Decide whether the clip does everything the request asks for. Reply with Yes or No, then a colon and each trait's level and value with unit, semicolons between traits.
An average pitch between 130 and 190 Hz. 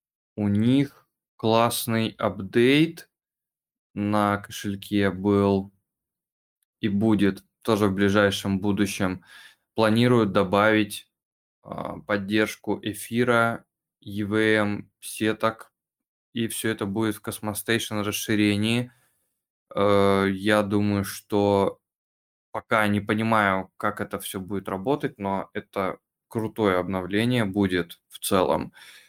No: low, 105 Hz